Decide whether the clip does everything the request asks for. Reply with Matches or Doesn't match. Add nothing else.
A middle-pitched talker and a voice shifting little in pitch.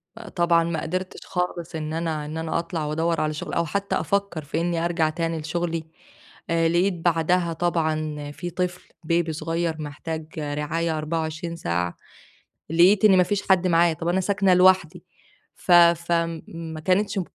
Matches